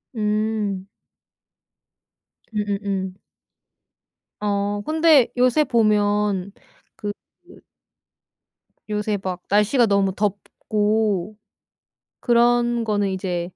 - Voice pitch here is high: Yes, high, 210 Hz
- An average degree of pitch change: No, narrow, 1.9 semitones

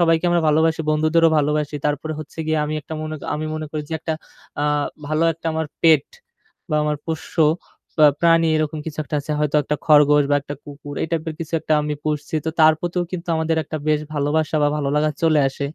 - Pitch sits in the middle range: Yes, medium, 155 Hz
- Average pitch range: No, narrow, 1.4 semitones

